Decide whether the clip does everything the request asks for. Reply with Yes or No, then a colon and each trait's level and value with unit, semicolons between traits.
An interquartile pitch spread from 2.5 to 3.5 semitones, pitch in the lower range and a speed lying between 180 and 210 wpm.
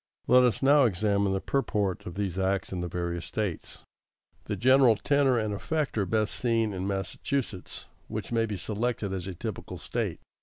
No: average, 4.4 semitones; low, 105 Hz; average, 185 wpm